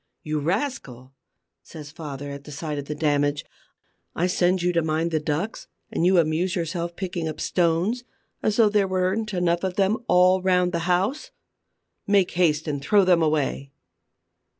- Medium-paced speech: Yes, average, 165 wpm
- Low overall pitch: No, medium, 170 Hz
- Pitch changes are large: No, average, 3.5 semitones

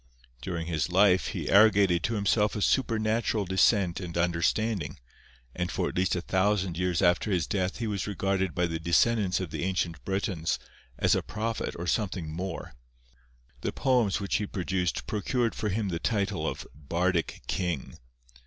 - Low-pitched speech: Yes, very low, 95 Hz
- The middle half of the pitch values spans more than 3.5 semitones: No, average, 3.2 semitones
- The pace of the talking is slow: No, average, 165 wpm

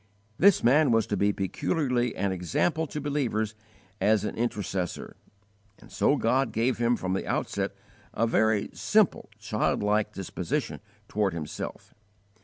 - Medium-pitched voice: No, low, 110 Hz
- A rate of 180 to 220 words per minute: No, slow, 135 wpm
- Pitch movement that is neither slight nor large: Yes, average, 4.4 semitones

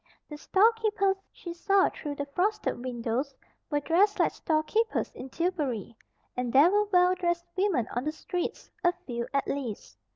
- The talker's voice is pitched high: Yes, very high, 335 Hz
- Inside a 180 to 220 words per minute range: No, average, 160 wpm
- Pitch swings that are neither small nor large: No, wide, 6.2 semitones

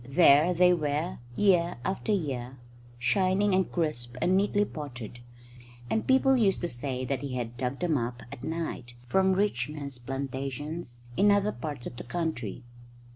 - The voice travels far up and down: Yes, wide, 6.7 semitones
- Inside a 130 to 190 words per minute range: Yes, average, 160 wpm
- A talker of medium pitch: Yes, medium, 150 Hz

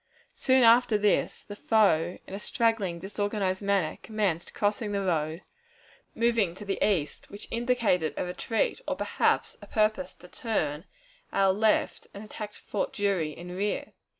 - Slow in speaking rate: No, average, 150 wpm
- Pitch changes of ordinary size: Yes, average, 3.4 semitones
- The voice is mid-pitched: No, high, 205 Hz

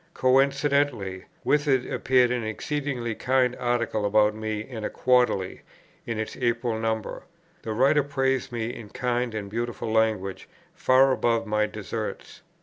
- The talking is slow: No, average, 145 wpm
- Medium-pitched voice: No, low, 120 Hz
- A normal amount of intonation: Yes, average, 3.1 semitones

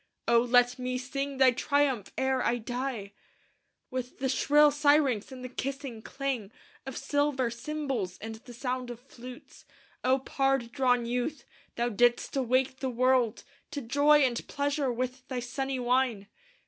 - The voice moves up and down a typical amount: No, narrow, 2.1 semitones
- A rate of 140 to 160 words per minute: Yes, average, 150 wpm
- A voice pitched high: Yes, very high, 255 Hz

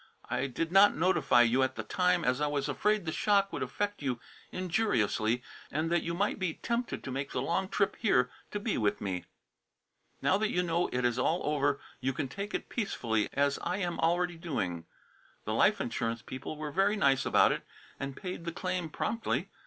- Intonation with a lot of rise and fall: Yes, wide, 6.2 semitones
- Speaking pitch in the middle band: Yes, medium, 165 Hz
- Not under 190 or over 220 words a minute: Yes, average, 200 wpm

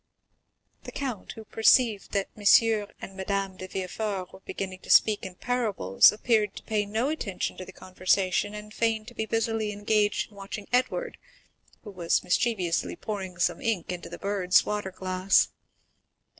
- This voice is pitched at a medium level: No, high, 205 Hz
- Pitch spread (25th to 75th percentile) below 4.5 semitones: Yes, average, 2.7 semitones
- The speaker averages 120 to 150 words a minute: No, average, 160 wpm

